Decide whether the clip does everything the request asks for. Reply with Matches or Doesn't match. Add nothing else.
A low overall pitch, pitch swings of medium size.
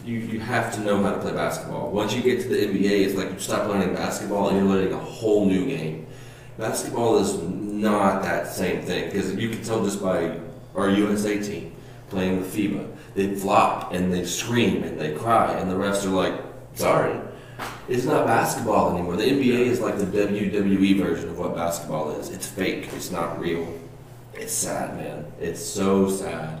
Doesn't match